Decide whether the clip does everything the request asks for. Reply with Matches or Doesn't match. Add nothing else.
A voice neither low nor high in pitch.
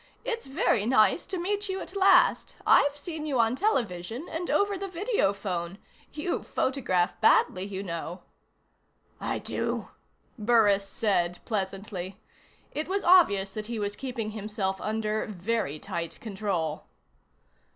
Doesn't match